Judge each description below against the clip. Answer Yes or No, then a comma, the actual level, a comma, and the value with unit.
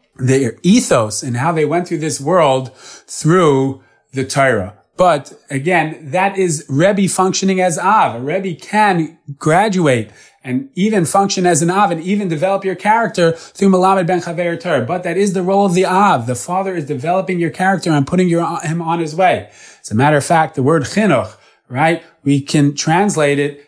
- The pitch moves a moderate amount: Yes, average, 4.5 semitones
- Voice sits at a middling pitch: Yes, medium, 170 Hz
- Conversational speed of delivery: Yes, average, 190 wpm